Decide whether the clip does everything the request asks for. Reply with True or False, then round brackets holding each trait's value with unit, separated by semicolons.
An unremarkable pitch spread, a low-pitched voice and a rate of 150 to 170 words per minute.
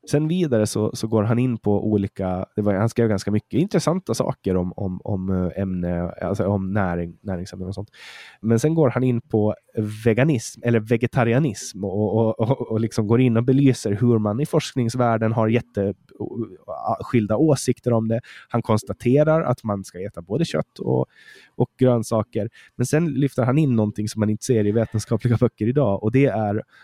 False (3.3 semitones; 115 Hz; 185 wpm)